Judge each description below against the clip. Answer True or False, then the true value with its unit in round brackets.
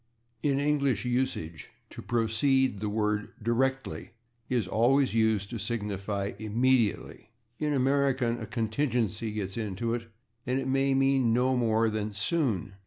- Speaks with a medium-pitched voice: False (115 Hz)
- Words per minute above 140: False (135 wpm)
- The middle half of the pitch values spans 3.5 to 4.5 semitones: True (3.8 semitones)